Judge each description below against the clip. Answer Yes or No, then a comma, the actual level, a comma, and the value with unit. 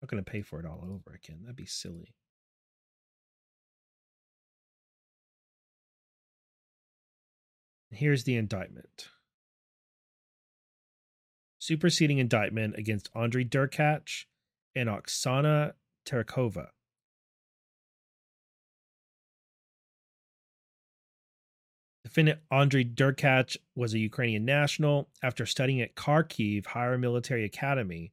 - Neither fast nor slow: No, slow, 80 wpm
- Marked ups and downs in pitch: No, average, 4.6 semitones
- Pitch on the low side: Yes, low, 125 Hz